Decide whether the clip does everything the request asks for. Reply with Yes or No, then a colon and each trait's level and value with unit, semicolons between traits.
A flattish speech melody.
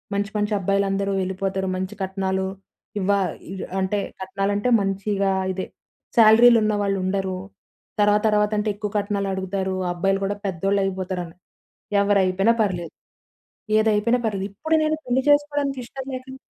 Yes: narrow, 1.8 semitones